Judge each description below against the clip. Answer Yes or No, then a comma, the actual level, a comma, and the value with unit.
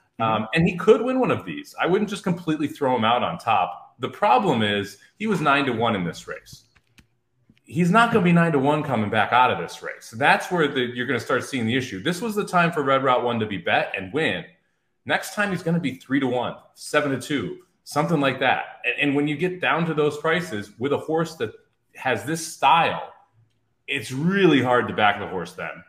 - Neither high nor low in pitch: Yes, medium, 145 Hz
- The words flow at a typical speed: No, fast, 240 wpm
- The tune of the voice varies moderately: No, wide, 6.0 semitones